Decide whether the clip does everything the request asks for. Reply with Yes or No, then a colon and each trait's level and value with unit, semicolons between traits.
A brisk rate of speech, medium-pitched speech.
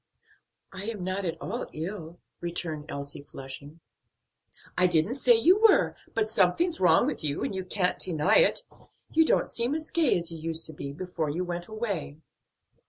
No: average, 170 wpm; medium, 180 Hz